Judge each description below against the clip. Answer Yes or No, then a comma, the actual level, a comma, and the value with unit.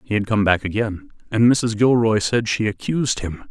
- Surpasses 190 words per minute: Yes, fast, 205 wpm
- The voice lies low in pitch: Yes, low, 110 Hz